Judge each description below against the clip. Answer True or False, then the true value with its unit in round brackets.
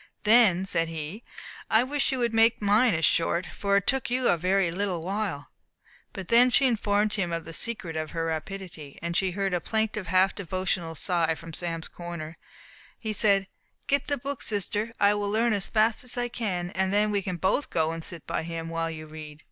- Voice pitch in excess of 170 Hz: True (190 Hz)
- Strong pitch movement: False (4.7 semitones)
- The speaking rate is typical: False (210 wpm)